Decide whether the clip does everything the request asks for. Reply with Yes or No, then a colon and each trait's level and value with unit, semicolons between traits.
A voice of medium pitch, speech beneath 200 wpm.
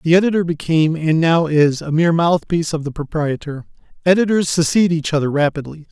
Yes: medium, 160 Hz; average, 170 wpm